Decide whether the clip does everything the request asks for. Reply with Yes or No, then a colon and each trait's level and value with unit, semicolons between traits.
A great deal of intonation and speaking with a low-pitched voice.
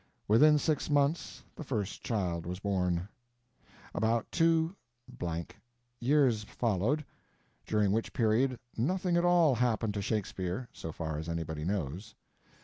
Yes: wide, 7.6 semitones; low, 110 Hz